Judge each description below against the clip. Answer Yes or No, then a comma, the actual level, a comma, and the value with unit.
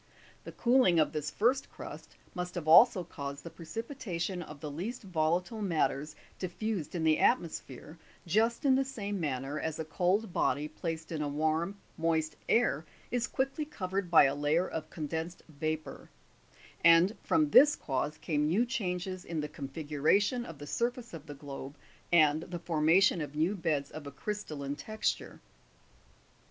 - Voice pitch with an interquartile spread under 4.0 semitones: No, average, 5.1 semitones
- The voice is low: No, medium, 165 Hz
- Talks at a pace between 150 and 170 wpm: Yes, average, 165 wpm